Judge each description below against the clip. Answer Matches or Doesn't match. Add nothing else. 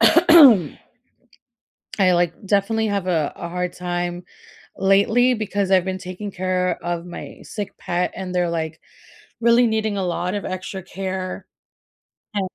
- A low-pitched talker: Doesn't match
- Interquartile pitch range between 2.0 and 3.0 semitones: Matches